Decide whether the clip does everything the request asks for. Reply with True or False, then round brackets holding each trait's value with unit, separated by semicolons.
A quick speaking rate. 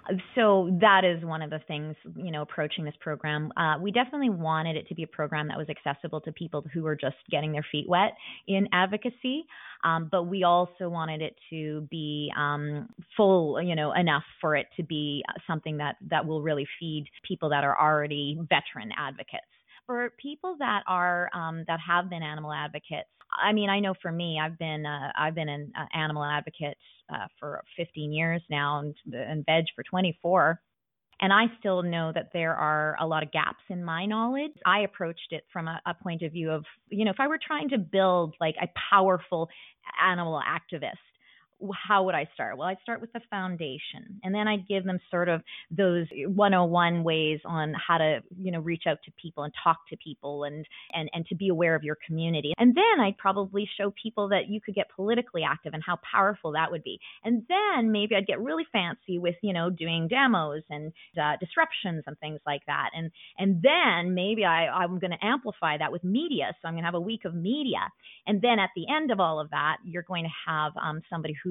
True (210 wpm)